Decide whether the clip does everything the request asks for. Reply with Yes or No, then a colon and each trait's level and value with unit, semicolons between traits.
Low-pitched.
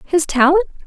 No: very high, 290 Hz